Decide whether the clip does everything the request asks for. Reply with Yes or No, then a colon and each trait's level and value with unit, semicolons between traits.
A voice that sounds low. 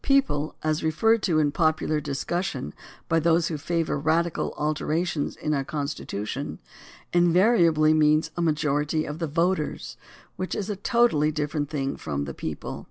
No: medium, 155 Hz